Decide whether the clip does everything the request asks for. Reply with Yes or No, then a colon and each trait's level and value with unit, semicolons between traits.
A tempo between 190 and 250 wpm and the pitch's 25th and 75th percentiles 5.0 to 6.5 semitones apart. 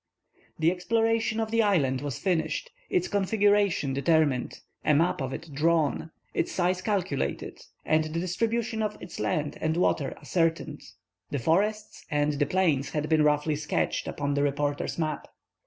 No: average, 155 wpm; wide, 5.6 semitones